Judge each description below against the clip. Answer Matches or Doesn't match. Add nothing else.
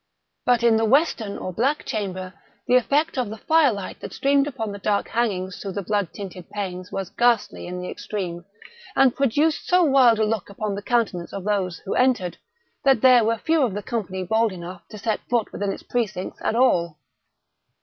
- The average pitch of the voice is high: Matches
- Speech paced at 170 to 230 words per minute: Matches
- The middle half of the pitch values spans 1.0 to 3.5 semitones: Doesn't match